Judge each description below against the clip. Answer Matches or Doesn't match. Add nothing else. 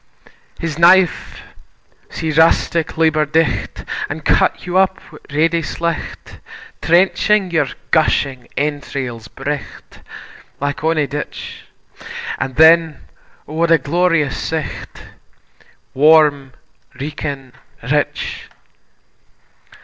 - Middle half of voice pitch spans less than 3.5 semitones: Matches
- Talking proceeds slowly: Matches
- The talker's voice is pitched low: Doesn't match